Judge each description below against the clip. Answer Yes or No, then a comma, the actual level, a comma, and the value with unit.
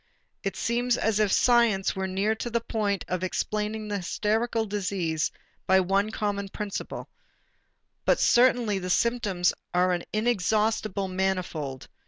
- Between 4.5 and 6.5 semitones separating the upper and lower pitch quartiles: No, average, 2.9 semitones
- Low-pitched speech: No, high, 205 Hz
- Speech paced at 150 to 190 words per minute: No, slow, 135 wpm